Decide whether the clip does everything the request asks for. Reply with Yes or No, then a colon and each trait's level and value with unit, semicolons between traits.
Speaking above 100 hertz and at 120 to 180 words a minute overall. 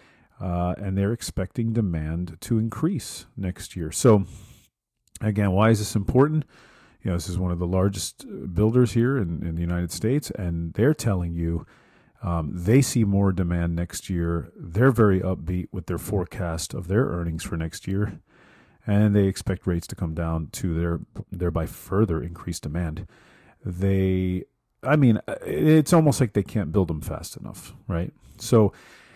No: very low, 95 Hz; average, 165 wpm